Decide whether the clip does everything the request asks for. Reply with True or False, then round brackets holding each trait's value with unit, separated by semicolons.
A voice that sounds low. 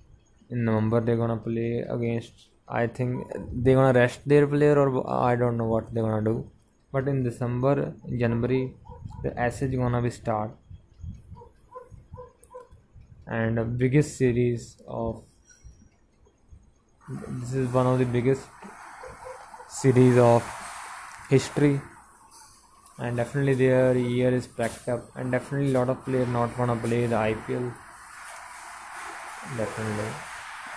True (120 Hz)